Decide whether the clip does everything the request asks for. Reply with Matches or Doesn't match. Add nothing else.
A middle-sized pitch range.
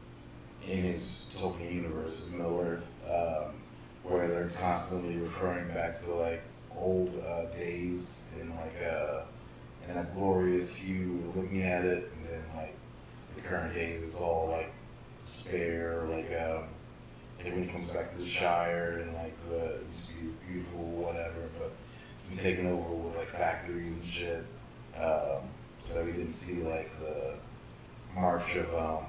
Doesn't match